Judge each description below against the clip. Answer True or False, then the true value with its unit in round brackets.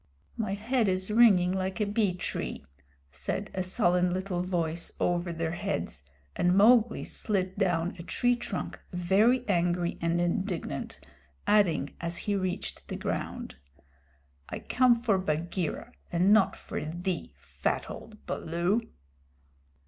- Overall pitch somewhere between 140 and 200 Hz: True (185 Hz)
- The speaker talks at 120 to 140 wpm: True (135 wpm)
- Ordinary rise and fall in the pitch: True (3.2 semitones)